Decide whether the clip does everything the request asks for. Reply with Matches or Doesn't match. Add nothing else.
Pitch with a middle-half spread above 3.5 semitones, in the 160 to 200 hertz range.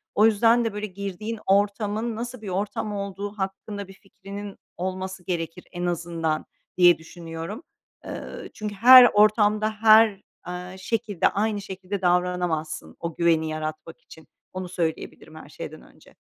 Doesn't match